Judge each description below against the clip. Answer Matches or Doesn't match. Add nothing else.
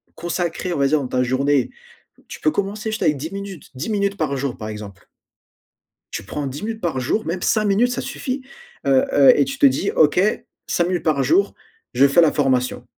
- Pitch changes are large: Matches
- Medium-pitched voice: Matches